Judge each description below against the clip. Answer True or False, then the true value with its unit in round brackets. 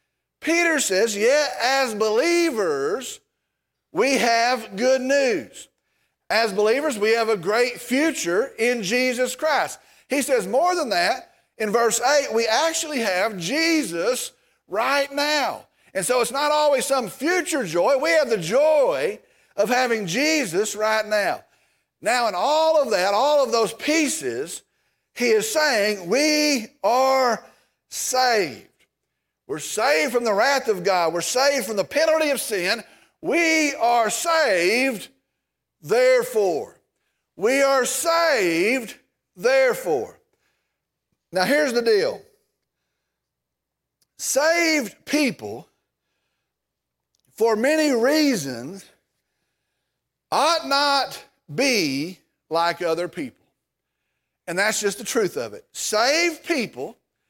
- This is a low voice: False (275 Hz)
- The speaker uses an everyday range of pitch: False (5.9 semitones)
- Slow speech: True (115 wpm)